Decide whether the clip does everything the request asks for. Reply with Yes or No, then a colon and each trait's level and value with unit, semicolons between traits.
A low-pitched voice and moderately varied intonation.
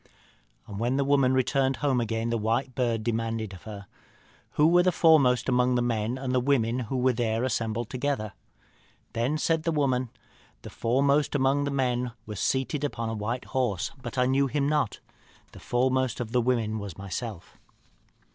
Yes: low, 125 Hz; average, 3.0 semitones